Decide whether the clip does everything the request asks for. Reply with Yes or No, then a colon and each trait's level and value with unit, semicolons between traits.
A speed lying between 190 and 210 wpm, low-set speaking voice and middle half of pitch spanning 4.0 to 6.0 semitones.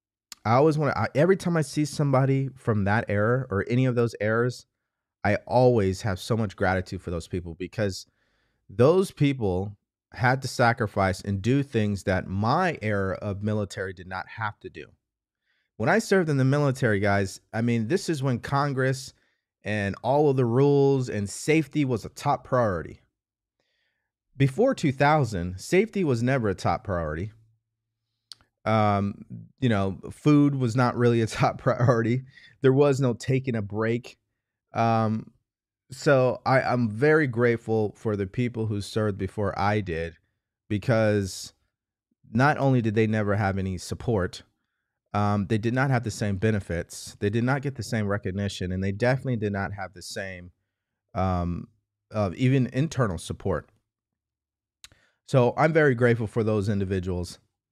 No: average, 155 wpm; low, 110 Hz; average, 4.4 semitones